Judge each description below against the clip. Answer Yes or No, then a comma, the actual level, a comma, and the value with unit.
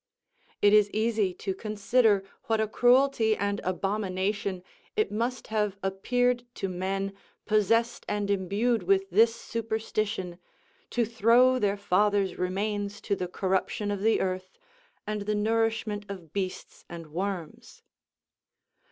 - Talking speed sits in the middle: No, slow, 125 wpm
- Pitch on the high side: Yes, high, 205 Hz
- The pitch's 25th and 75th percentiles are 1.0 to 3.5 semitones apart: Yes, narrow, 2.5 semitones